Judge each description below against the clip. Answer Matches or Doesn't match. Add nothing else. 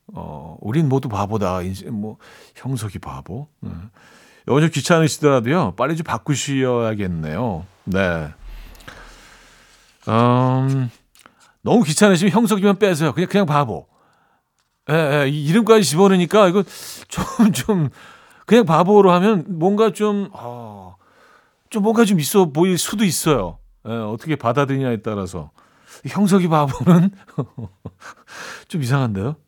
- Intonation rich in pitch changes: Matches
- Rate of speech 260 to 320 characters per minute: Doesn't match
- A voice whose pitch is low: Doesn't match